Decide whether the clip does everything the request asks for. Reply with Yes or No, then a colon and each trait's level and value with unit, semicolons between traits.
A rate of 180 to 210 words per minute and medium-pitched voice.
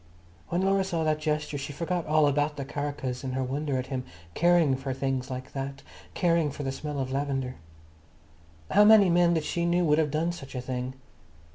Yes: average, 195 wpm; medium, 145 Hz